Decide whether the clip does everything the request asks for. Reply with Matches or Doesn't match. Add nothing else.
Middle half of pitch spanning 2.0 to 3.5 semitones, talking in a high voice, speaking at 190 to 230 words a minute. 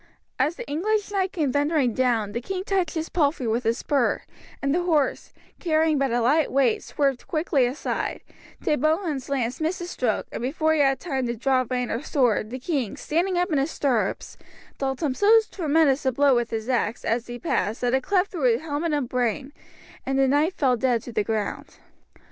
Doesn't match